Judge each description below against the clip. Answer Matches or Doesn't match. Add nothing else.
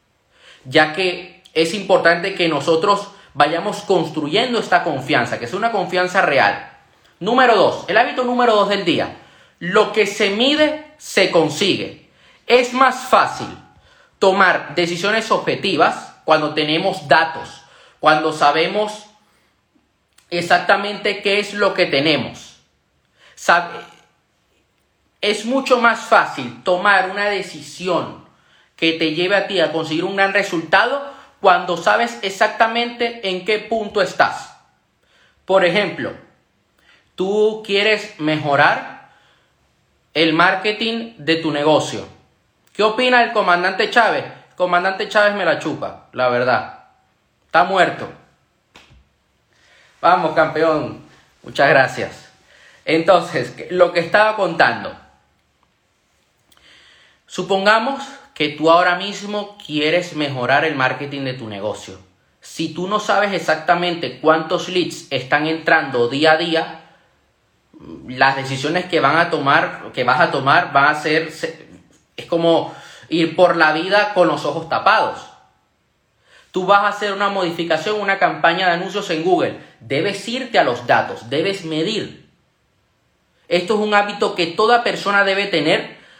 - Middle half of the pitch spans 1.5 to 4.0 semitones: Doesn't match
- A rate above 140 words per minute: Doesn't match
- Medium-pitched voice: Matches